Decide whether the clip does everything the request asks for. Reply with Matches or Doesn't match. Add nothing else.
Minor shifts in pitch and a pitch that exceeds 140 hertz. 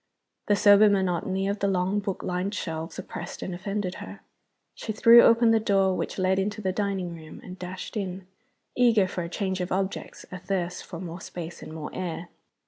Matches